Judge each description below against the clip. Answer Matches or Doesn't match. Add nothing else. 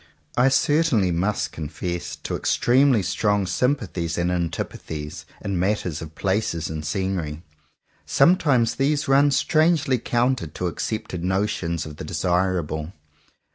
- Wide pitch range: Matches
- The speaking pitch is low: Matches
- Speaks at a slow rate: Matches